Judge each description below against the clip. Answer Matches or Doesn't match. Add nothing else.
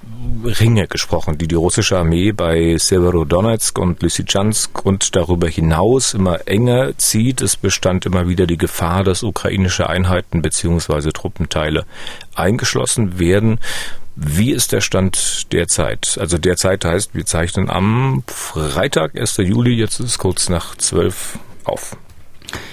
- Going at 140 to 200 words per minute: Doesn't match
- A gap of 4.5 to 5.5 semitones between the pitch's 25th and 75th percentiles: Doesn't match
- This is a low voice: Matches